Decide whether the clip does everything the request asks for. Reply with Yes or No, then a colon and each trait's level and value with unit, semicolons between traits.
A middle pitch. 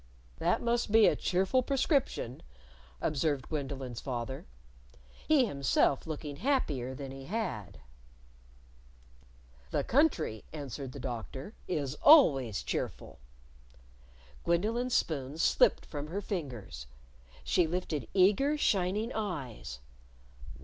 Yes: medium, 155 Hz